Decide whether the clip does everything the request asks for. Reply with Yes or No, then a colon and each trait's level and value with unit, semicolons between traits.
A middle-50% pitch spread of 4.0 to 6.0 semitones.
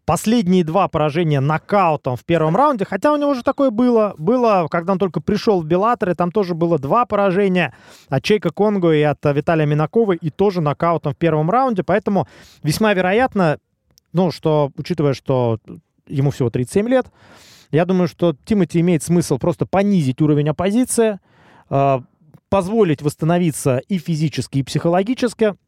Yes: average, 5.1 semitones